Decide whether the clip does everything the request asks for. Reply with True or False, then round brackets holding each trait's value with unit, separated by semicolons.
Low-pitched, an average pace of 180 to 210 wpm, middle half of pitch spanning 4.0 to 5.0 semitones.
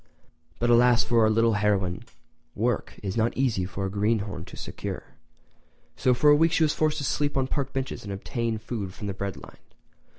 True (115 Hz; 195 wpm; 4.6 semitones)